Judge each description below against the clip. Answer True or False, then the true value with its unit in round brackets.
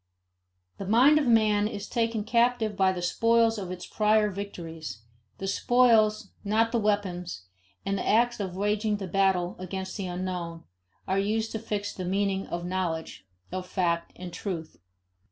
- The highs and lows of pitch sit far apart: False (3.1 semitones)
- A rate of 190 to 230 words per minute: False (160 wpm)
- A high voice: True (200 Hz)